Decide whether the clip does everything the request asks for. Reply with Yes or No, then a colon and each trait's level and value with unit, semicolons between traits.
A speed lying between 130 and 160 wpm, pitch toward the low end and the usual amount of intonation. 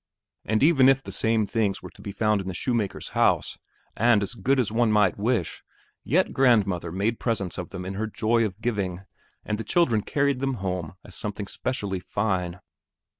No: average, 190 wpm; low, 105 Hz; average, 3.8 semitones